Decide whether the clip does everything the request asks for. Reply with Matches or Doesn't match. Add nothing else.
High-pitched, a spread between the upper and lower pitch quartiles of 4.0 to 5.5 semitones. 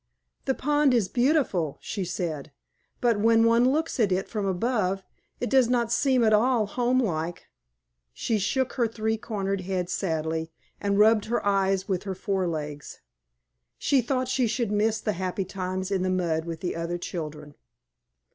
Matches